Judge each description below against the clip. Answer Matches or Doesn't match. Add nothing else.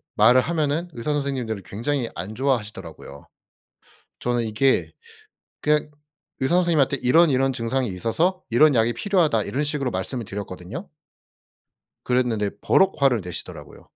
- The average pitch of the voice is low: Matches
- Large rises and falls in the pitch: Doesn't match